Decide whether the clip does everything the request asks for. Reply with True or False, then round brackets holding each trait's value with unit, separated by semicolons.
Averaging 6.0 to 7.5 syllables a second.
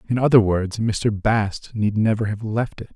False (4.5 syllables/s)